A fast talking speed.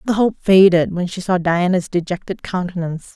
No: average, 190 wpm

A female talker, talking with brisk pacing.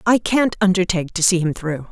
Yes: female; fast, 220 wpm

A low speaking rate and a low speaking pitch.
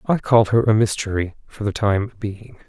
No: average, 200 wpm; low, 105 Hz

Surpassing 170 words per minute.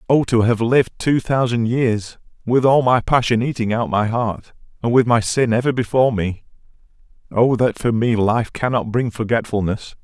Yes: average, 180 wpm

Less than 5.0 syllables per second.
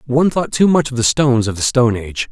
No: 6.9 syllables/s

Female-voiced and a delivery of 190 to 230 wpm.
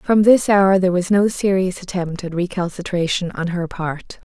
No: female; average, 180 wpm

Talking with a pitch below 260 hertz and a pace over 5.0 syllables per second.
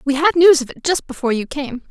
No: very high, 285 Hz; 6.2 syllables/s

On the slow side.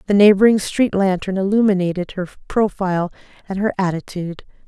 Yes: slow, 130 wpm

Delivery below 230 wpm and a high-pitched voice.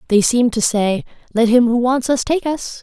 No: fast, 235 wpm; high, 240 Hz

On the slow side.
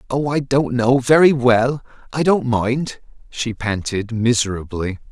Yes: slow, 130 wpm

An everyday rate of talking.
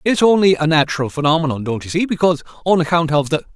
No: fast, 220 wpm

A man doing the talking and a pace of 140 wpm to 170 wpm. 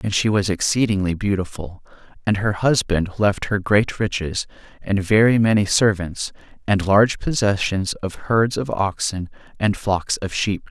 Yes: male; average, 150 wpm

